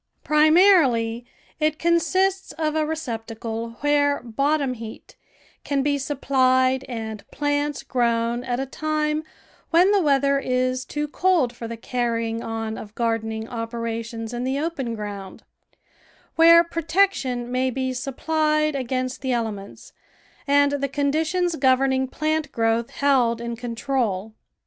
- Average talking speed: No, slow, 130 wpm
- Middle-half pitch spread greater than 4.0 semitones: Yes, average, 4.6 semitones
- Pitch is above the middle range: Yes, very high, 260 Hz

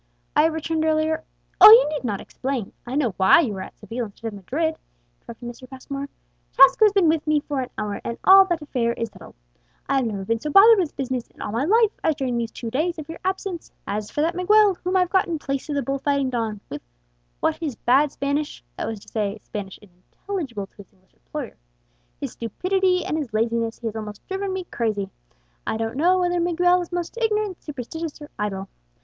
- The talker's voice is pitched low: No, very high, 280 Hz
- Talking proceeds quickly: Yes, fast, 225 wpm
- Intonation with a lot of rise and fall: Yes, wide, 7.2 semitones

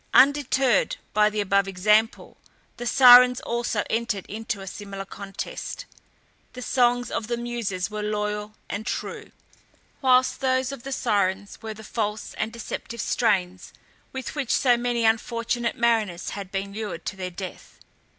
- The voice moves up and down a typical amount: Yes, average, 3.2 semitones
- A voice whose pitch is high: Yes, high, 220 Hz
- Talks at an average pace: Yes, average, 150 wpm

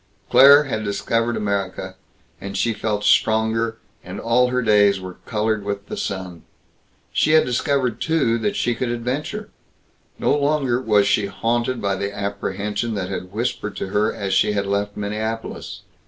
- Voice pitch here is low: Yes, low, 110 Hz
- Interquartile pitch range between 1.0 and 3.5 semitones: Yes, average, 3.2 semitones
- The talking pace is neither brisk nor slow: Yes, average, 160 wpm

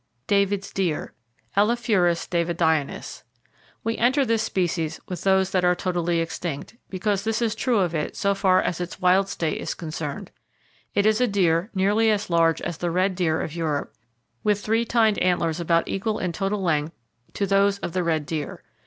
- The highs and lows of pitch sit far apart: No, average, 3.4 semitones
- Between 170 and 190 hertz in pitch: Yes, medium, 185 Hz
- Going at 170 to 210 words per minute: Yes, average, 180 wpm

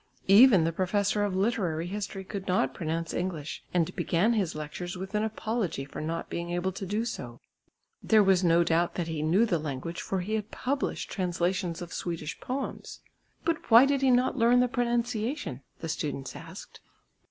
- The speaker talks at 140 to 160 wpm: No, average, 180 wpm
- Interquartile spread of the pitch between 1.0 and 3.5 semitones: No, average, 4.8 semitones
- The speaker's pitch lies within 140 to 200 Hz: Yes, medium, 185 Hz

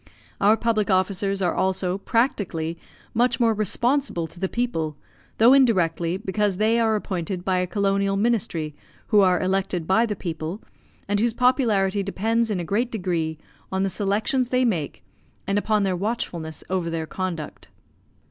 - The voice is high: Yes, high, 195 Hz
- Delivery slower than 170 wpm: Yes, average, 155 wpm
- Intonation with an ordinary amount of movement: Yes, average, 3.7 semitones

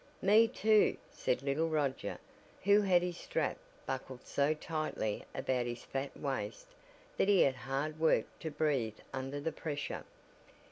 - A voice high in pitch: No, medium, 145 Hz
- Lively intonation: No, average, 3.7 semitones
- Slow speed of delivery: No, average, 145 wpm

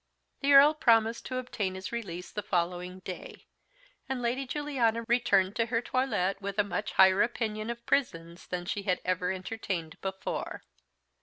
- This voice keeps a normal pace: Yes, average, 160 wpm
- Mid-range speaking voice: No, high, 210 Hz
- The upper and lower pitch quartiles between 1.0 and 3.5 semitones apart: No, average, 4.3 semitones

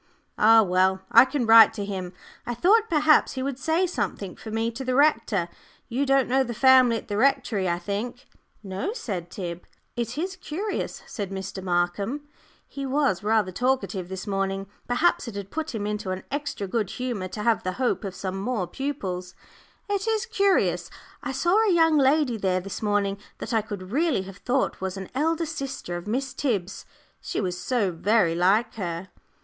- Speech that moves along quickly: No, average, 190 wpm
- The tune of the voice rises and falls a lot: Yes, wide, 6.2 semitones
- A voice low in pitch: No, high, 225 Hz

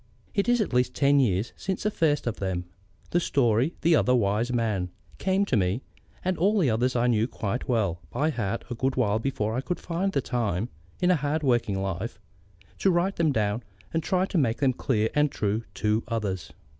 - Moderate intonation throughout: No, wide, 6.6 semitones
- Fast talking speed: Yes, fast, 210 wpm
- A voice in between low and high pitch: No, low, 125 Hz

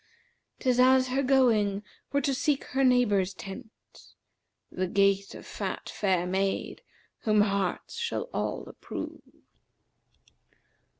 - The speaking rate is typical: No, slow, 120 wpm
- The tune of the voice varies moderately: Yes, average, 4.9 semitones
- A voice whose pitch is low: No, high, 220 Hz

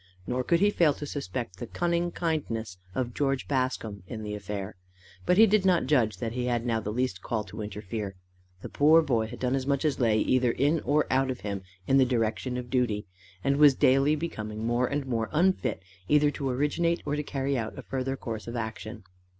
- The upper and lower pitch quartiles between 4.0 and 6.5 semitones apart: Yes, average, 4.6 semitones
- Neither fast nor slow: No, fast, 210 wpm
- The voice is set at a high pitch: No, low, 130 Hz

